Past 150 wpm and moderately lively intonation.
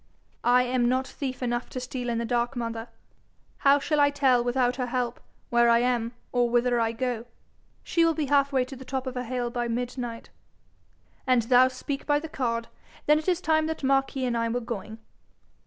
No: fast, 205 wpm; narrow, 2.1 semitones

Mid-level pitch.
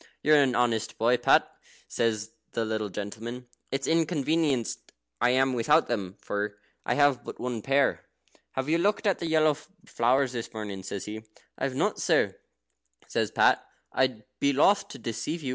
No: low, 125 Hz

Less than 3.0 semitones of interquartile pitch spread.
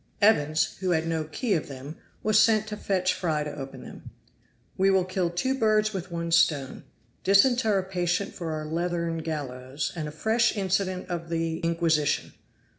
No: average, 3.7 semitones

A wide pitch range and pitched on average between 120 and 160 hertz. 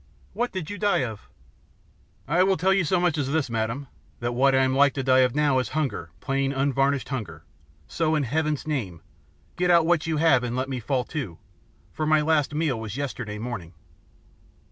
No: average, 4.1 semitones; medium, 140 Hz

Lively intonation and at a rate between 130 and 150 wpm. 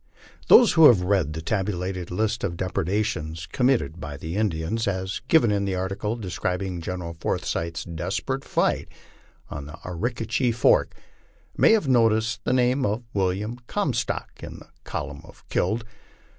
No: average, 4.8 semitones; average, 145 wpm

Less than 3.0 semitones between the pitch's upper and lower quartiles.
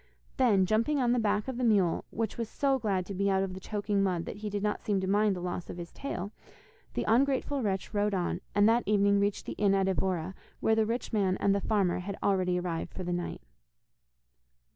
Yes: narrow, 2.5 semitones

